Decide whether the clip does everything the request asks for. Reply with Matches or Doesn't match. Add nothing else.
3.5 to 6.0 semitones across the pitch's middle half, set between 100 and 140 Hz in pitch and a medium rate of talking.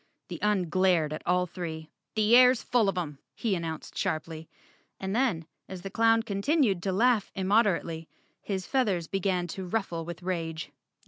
Doesn't match